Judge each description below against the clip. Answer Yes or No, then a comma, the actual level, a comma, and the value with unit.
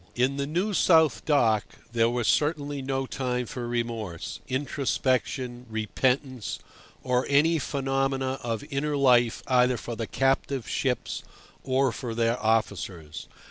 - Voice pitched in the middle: No, low, 130 Hz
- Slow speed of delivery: Yes, slow, 130 wpm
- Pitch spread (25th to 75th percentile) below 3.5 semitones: Yes, average, 2.8 semitones